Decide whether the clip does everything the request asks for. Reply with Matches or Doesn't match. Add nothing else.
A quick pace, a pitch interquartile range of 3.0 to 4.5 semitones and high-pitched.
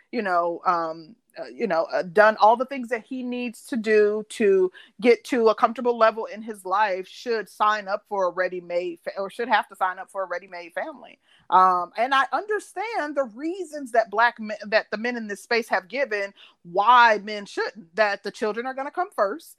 Matches